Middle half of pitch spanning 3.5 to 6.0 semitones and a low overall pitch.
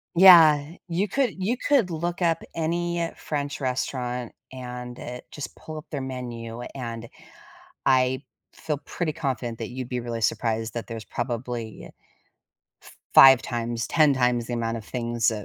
Yes: average, 4.9 semitones; low, 125 Hz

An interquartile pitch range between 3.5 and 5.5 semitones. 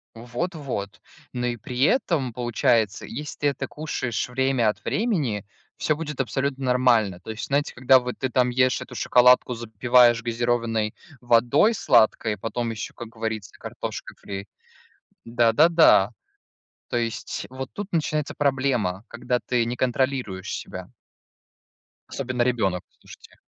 No: average, 2.9 semitones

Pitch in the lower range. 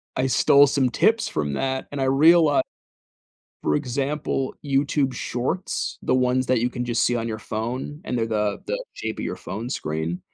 Yes: low, 130 Hz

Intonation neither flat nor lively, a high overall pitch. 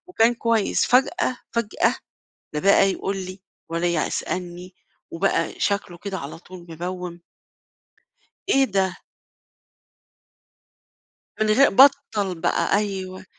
Yes: average, 3.4 semitones; high, 195 Hz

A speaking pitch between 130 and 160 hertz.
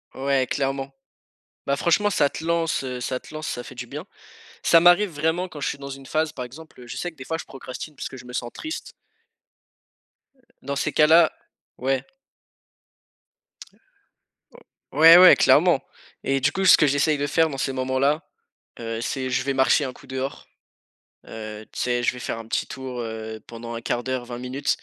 Yes: low, 135 Hz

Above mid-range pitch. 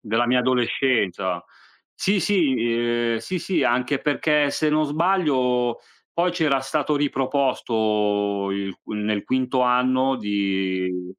No: low, 125 Hz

